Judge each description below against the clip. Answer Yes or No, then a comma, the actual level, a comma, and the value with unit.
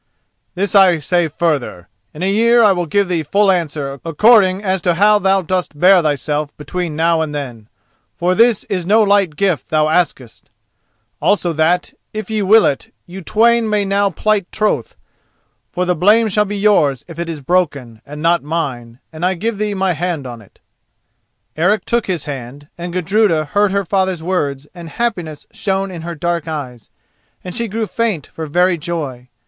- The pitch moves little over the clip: No, average, 4.6 semitones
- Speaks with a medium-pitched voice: Yes, medium, 175 Hz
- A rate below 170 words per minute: No, average, 185 wpm